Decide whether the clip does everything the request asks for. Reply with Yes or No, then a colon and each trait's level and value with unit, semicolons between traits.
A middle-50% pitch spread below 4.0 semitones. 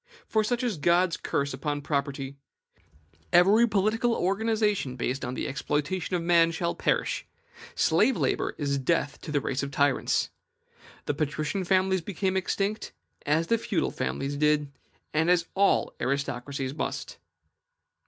No: wide, 5.5 semitones